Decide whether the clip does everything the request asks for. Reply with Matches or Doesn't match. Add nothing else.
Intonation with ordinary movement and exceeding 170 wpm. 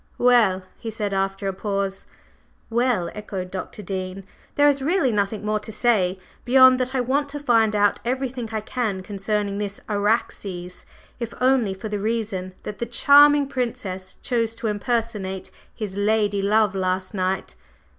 Doesn't match